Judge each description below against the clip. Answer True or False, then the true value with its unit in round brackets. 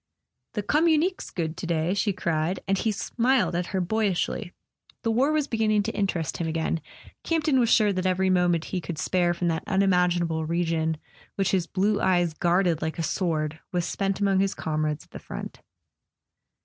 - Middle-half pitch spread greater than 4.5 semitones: False (3.6 semitones)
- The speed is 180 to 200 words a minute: True (185 wpm)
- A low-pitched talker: False (185 Hz)